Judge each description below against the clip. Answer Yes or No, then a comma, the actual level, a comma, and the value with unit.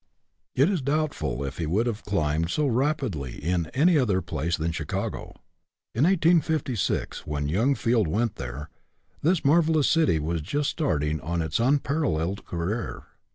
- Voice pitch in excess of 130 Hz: No, low, 105 Hz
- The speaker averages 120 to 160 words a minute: Yes, average, 155 wpm